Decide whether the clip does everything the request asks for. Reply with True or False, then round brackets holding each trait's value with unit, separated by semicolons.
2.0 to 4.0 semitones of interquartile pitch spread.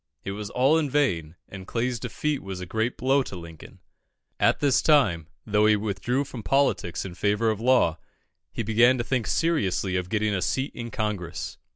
False (5.2 semitones)